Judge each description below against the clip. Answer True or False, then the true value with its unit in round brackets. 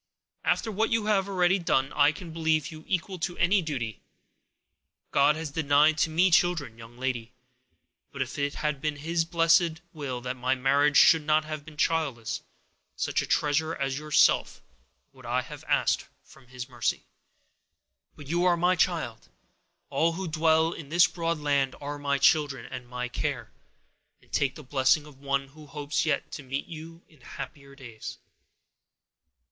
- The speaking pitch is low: False (150 Hz)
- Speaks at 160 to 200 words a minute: True (170 wpm)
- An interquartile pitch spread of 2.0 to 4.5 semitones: True (3.3 semitones)